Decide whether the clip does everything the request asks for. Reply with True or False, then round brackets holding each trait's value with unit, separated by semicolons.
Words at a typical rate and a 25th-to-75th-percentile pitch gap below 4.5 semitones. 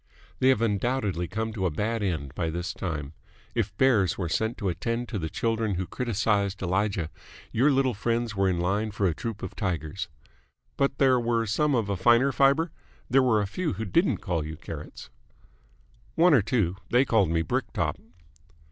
False (190 wpm; 4.8 semitones)